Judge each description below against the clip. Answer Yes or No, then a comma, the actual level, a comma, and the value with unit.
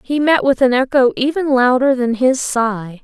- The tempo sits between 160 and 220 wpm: Yes, average, 200 wpm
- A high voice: Yes, very high, 255 Hz